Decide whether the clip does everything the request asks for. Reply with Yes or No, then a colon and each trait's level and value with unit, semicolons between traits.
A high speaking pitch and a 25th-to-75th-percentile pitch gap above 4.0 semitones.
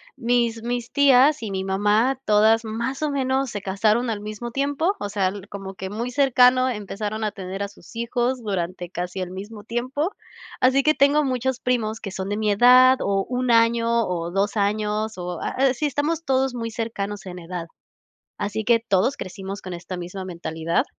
Yes: high, 220 Hz; average, 4.4 semitones